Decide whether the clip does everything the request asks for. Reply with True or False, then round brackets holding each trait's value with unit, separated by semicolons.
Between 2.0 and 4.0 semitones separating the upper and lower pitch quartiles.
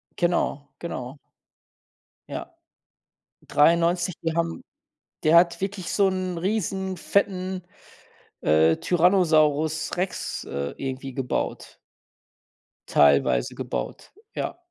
False (5.1 semitones)